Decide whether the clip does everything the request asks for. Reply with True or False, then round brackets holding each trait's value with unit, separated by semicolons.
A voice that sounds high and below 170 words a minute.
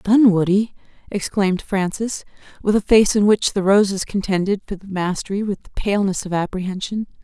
True (195 Hz; 160 wpm)